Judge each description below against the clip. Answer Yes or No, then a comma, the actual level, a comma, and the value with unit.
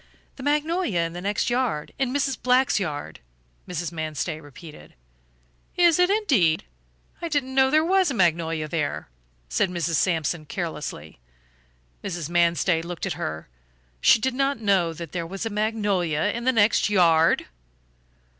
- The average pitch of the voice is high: No, medium, 180 Hz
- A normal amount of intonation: No, wide, 8.0 semitones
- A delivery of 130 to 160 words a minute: Yes, average, 150 wpm